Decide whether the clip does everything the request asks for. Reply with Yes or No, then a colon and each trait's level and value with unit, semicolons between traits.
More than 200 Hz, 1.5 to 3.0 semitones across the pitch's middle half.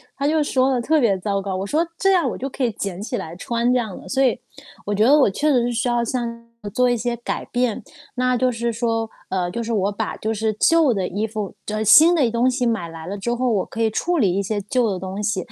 No: high, 230 Hz; average, 3.8 semitones